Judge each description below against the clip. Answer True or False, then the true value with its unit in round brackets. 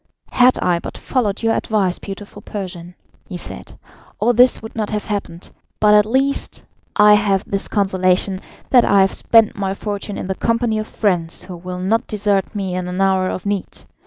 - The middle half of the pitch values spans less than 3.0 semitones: True (2.5 semitones)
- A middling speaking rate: True (190 wpm)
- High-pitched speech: True (200 Hz)